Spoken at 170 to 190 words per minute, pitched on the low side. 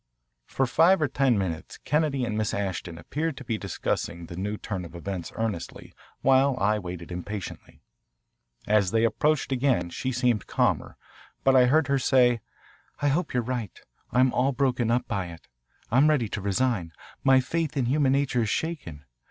Yes: average, 175 wpm; low, 120 Hz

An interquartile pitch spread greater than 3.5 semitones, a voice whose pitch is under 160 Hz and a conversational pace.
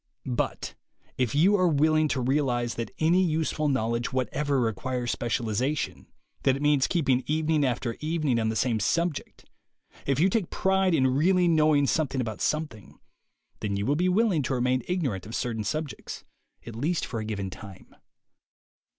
Yes: average, 5.0 semitones; low, 135 Hz; average, 165 wpm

